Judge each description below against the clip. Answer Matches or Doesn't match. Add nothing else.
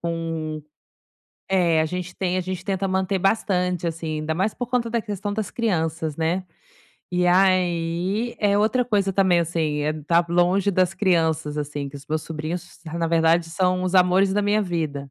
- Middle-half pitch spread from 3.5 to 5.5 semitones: Doesn't match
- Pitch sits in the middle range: Matches